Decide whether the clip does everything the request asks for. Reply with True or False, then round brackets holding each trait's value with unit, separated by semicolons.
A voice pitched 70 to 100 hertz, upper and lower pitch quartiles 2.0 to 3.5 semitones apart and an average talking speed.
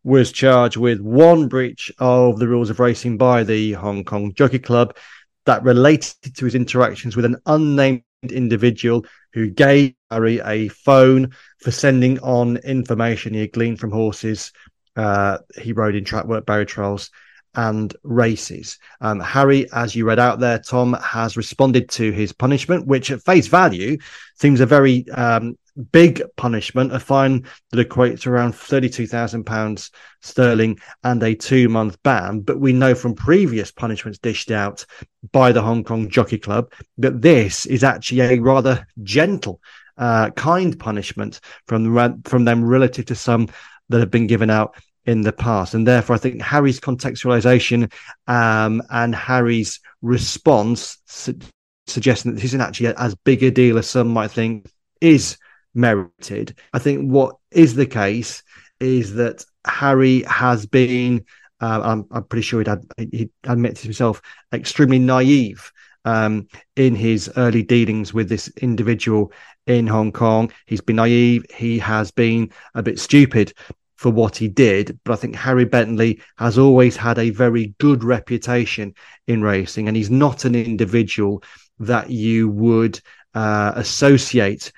False (120 Hz; 2.4 semitones; 155 wpm)